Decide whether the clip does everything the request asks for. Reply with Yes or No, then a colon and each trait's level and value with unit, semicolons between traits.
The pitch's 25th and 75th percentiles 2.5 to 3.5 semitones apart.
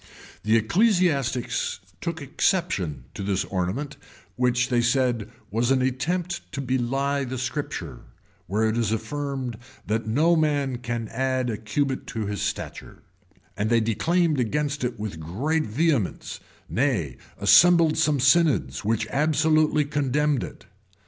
No: average, 5.1 semitones